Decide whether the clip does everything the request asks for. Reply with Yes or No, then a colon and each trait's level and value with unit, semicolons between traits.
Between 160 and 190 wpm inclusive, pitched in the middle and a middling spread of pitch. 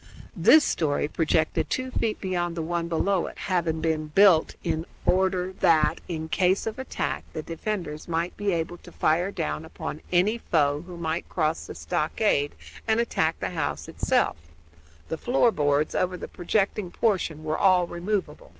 Yes: average, 170 wpm; medium, 175 Hz; average, 3.4 semitones